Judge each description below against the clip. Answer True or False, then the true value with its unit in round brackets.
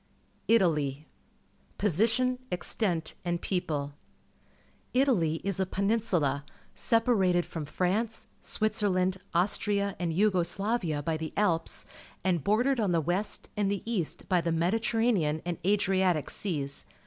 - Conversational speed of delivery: False (130 wpm)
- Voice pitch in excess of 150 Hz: True (185 Hz)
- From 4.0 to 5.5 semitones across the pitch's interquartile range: True (4.3 semitones)